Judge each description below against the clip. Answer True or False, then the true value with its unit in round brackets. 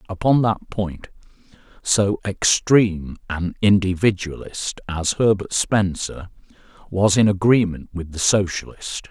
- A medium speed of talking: False (105 wpm)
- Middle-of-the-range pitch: False (95 Hz)